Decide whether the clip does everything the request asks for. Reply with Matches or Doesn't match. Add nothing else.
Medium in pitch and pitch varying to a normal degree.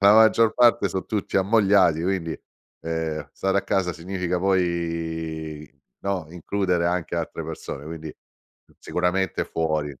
Doesn't match